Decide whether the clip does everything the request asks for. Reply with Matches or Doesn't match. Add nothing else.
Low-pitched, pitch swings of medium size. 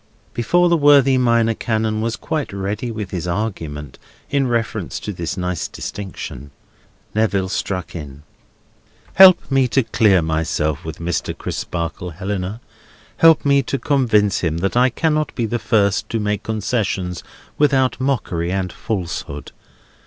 Doesn't match